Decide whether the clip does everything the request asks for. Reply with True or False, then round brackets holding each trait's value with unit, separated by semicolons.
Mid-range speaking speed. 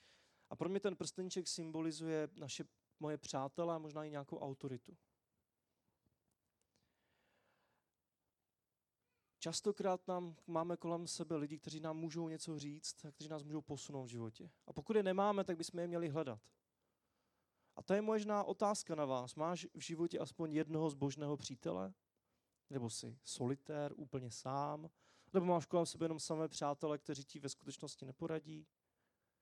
True (145 wpm)